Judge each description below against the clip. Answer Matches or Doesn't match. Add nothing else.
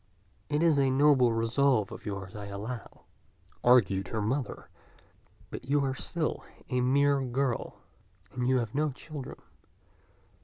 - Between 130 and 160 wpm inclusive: Matches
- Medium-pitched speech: Doesn't match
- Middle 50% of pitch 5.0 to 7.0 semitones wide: Doesn't match